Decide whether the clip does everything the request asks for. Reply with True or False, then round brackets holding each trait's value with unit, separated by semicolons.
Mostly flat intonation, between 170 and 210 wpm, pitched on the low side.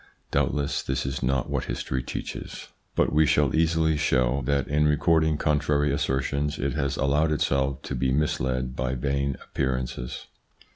False (2.2 semitones; 160 wpm; 70 Hz)